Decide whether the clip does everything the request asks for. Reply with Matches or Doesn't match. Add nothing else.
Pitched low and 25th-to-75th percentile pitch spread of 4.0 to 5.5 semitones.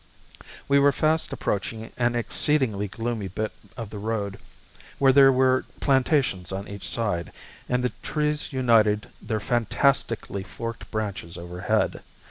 Matches